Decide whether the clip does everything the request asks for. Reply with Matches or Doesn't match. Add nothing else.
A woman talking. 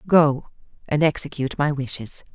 Matches